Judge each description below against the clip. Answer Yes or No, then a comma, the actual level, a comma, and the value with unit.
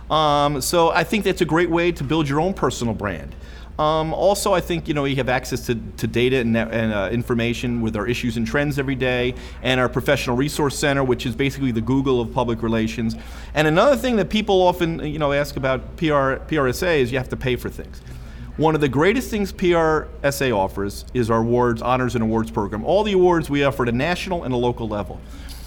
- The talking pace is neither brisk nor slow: No, fast, 220 wpm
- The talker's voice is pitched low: Yes, low, 130 Hz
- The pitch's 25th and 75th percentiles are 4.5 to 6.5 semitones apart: Yes, average, 5.2 semitones